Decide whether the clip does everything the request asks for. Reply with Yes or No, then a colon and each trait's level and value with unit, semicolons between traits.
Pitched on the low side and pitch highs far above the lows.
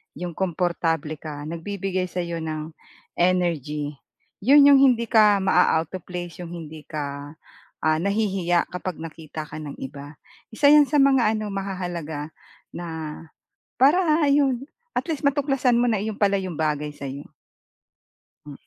No: medium, 180 Hz; wide, 6.0 semitones